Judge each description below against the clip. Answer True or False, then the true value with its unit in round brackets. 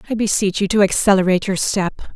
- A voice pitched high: True (195 Hz)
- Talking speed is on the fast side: False (195 wpm)